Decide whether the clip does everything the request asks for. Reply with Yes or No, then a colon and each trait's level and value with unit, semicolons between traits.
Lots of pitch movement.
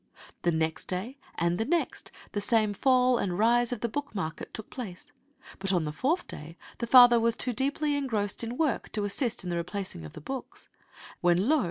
Yes: wide, 5.9 semitones